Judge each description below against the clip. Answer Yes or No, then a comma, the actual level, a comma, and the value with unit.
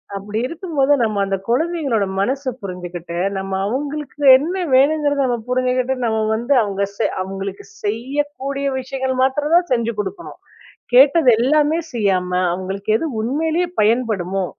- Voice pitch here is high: Yes, very high, 255 Hz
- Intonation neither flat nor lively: No, wide, 6.3 semitones